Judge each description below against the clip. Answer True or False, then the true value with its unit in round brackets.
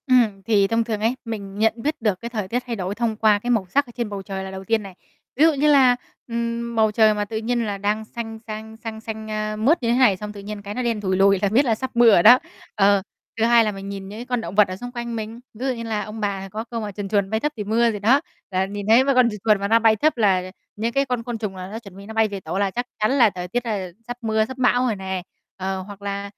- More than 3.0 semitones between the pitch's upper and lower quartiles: False (2.7 semitones)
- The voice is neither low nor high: False (220 Hz)